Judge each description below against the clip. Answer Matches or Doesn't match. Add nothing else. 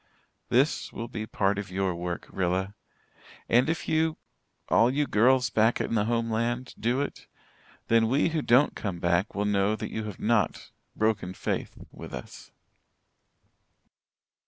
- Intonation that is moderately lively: Matches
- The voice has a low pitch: Matches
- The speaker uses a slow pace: Doesn't match